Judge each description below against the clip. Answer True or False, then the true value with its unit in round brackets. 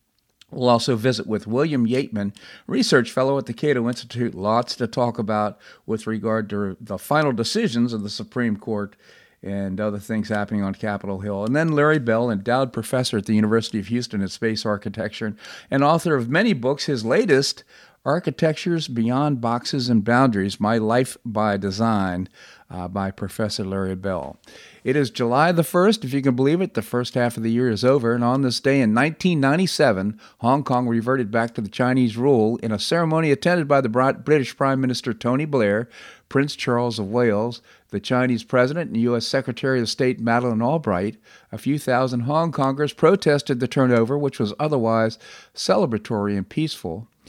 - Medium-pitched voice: False (120 Hz)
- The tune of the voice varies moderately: True (3.9 semitones)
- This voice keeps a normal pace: True (175 wpm)